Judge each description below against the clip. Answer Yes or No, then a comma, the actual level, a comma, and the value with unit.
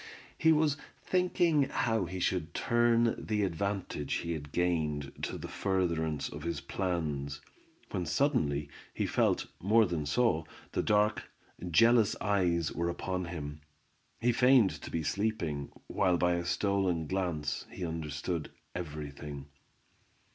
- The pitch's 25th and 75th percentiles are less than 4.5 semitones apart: No, average, 5.3 semitones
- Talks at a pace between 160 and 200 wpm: No, slow, 135 wpm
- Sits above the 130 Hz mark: No, very low, 90 Hz